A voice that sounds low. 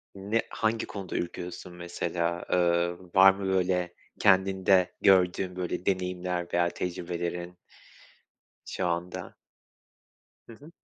Yes: very low, 90 Hz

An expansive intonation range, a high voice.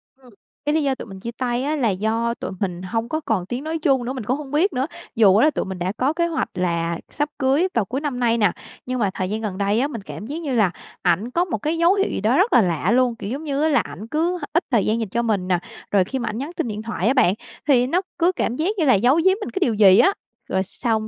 Yes: wide, 6.2 semitones; high, 240 Hz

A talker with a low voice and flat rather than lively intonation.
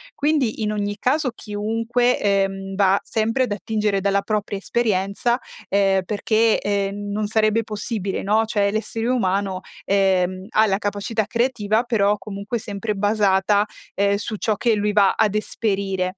No: high, 205 Hz; narrow, 1.9 semitones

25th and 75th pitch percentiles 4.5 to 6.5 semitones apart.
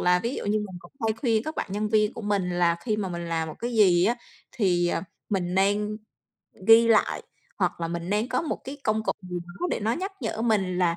No: average, 3.9 semitones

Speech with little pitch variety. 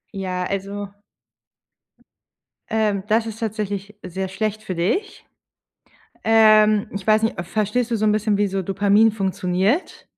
Yes: narrow, 2.0 semitones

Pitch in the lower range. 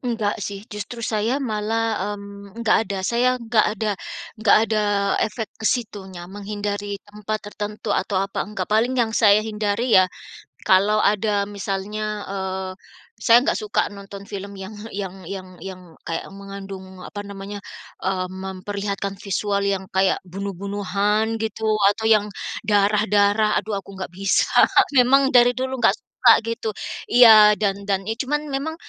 No: high, 205 Hz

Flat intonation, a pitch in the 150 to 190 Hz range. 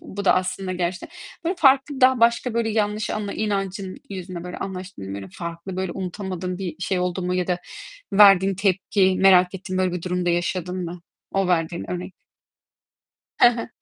Yes: narrow, 2.1 semitones; medium, 185 Hz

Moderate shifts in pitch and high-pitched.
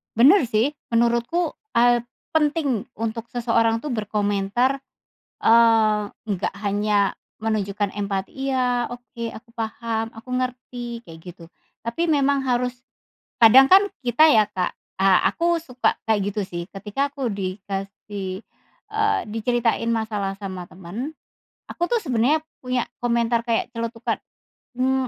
Yes: average, 3.5 semitones; high, 230 Hz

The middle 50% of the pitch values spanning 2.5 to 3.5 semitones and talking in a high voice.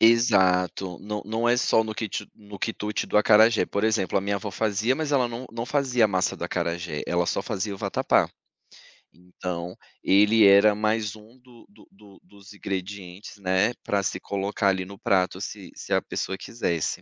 No: average, 2.8 semitones; low, 105 Hz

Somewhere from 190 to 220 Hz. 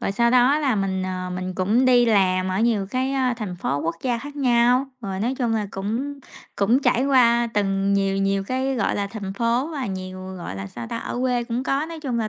No: high, 230 Hz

